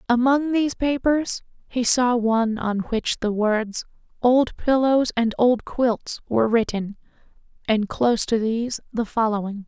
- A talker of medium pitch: No, high, 235 Hz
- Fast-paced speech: No, average, 145 wpm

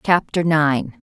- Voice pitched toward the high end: No, medium, 165 Hz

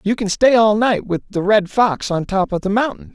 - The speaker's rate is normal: No, fast, 265 wpm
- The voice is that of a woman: No, male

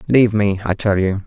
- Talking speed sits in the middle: No, fast, 235 wpm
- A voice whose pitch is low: Yes, low, 105 Hz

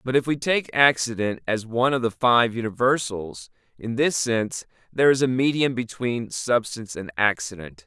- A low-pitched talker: Yes, low, 115 Hz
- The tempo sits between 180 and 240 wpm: No, average, 170 wpm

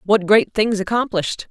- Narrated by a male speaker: No, female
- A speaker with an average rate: Yes, average, 160 wpm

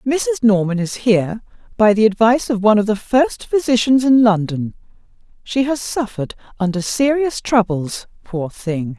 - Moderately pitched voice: No, high, 220 Hz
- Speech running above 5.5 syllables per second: No, 5.0 syllables/s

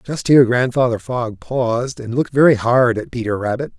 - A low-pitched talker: Yes, low, 120 Hz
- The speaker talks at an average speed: Yes, average, 190 wpm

